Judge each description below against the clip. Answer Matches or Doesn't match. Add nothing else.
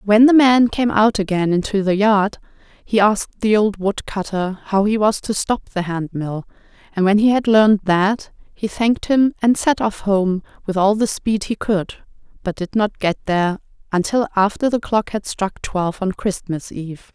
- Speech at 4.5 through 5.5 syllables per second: Matches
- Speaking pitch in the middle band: Doesn't match